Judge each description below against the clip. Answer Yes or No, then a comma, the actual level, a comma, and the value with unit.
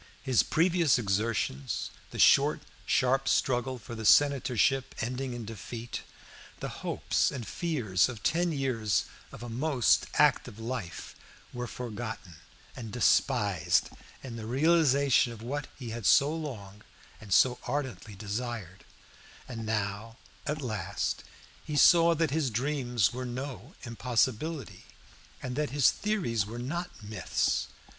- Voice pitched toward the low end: Yes, low, 125 Hz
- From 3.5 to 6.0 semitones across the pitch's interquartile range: Yes, average, 4.1 semitones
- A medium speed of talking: No, slow, 130 wpm